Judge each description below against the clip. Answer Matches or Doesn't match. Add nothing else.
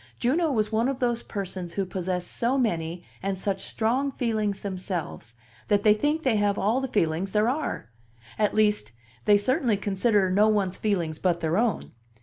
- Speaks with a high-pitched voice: Matches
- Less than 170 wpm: Doesn't match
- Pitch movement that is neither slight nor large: Matches